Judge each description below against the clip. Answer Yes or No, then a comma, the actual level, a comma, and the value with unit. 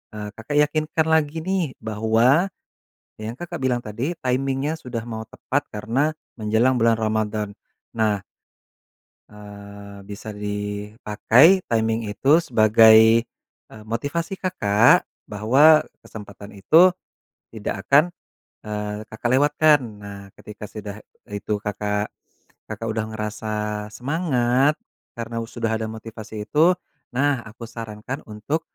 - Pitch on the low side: Yes, low, 110 Hz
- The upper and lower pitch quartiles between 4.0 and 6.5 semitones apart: Yes, average, 4.5 semitones